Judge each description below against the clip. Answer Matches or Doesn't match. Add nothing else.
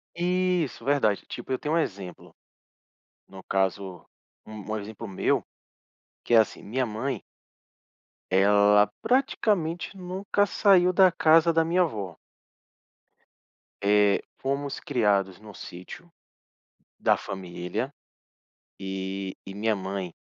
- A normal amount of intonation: Doesn't match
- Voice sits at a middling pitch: Doesn't match